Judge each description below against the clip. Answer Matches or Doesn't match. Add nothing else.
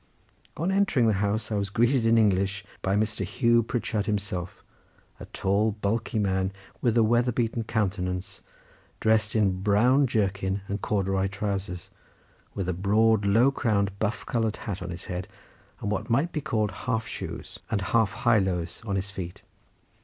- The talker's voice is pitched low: Matches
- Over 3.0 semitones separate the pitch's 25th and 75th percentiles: Doesn't match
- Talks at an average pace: Matches